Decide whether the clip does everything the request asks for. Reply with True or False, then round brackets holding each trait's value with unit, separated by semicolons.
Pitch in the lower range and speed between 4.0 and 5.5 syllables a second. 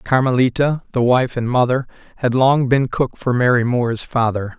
True (125 Hz; 4.9 syllables/s)